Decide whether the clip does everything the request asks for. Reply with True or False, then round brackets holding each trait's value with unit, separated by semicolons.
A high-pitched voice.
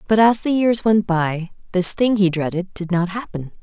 True (195 Hz)